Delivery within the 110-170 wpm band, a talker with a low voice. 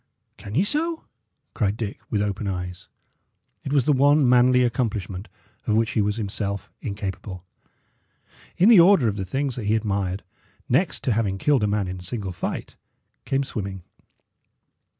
Yes: average, 160 wpm; low, 110 Hz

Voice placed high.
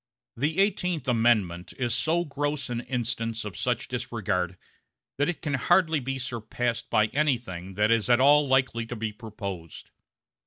No: low, 120 Hz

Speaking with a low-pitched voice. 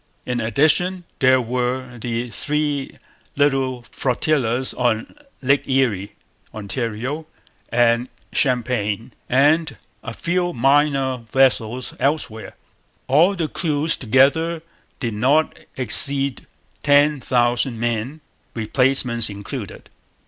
Yes: low, 130 Hz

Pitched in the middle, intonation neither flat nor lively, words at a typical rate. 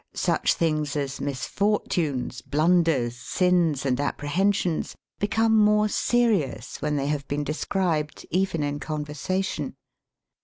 No: medium, 155 Hz; average, 4.9 semitones; slow, 115 wpm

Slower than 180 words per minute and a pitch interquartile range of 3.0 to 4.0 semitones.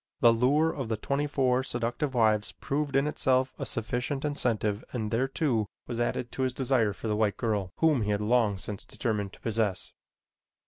No: average, 185 wpm; average, 3.7 semitones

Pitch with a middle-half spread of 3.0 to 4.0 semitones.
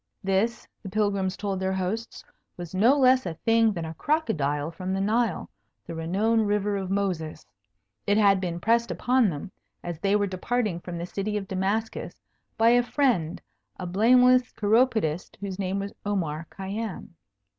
Yes: average, 3.7 semitones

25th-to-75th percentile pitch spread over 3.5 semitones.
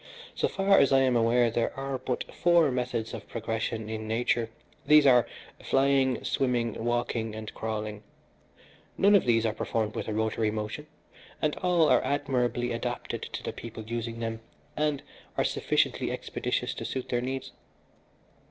No: average, 3.1 semitones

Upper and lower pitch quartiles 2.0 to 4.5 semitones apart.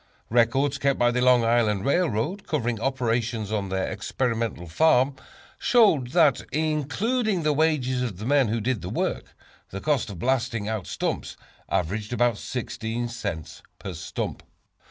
Yes: average, 4.2 semitones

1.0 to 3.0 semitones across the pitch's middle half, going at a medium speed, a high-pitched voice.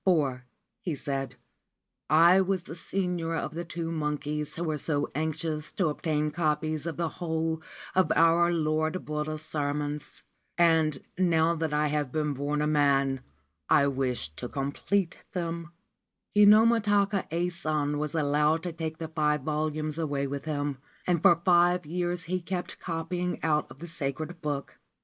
No: narrow, 2.5 semitones; average, 160 wpm; medium, 155 Hz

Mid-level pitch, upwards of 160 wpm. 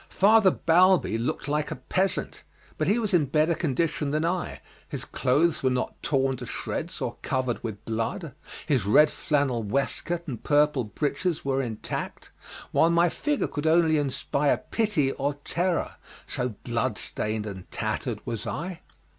No: medium, 150 Hz; average, 155 wpm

